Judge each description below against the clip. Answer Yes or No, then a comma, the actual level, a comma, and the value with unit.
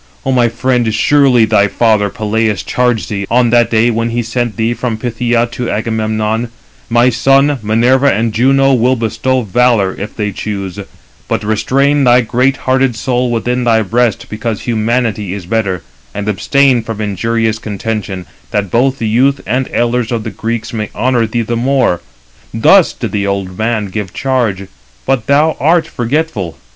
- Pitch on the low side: Yes, low, 115 Hz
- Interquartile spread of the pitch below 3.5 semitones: Yes, average, 2.7 semitones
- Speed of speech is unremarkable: Yes, average, 165 wpm